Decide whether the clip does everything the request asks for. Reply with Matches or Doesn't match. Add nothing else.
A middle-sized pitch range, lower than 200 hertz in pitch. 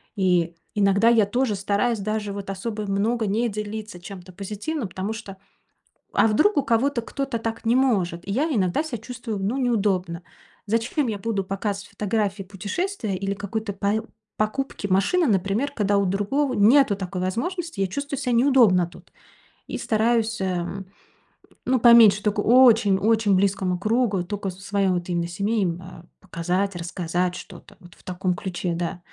Doesn't match